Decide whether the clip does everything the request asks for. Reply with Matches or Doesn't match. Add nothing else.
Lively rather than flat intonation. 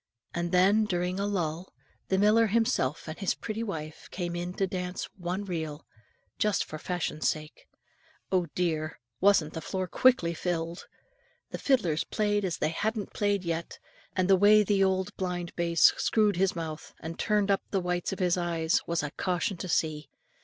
Doesn't match